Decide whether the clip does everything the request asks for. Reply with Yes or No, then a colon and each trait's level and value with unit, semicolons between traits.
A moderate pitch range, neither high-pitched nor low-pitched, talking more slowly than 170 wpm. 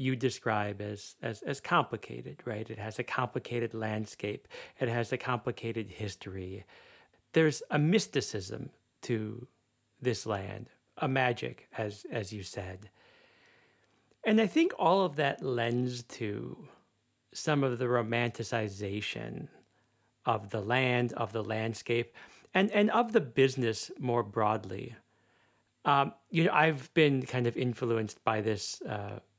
No: average, 3.6 semitones; low, 120 Hz; slow, 135 wpm